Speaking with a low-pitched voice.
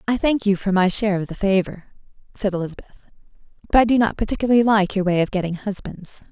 No: high, 200 Hz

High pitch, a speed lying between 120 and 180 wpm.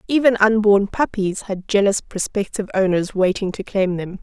Yes: high, 200 Hz; average, 155 wpm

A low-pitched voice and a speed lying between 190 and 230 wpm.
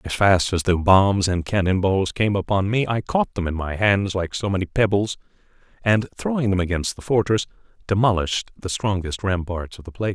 Yes: very low, 95 Hz; average, 200 wpm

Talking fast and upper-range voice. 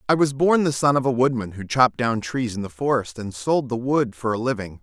No: fast, 275 wpm; low, 125 Hz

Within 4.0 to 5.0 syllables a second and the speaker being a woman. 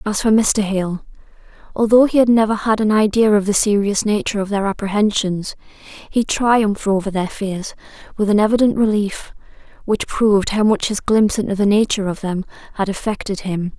No: 5.3 syllables/s; female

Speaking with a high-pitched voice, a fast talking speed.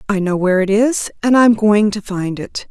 Yes: high, 210 Hz; fast, 265 wpm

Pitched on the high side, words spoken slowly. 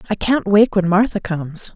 No: high, 195 Hz; fast, 205 wpm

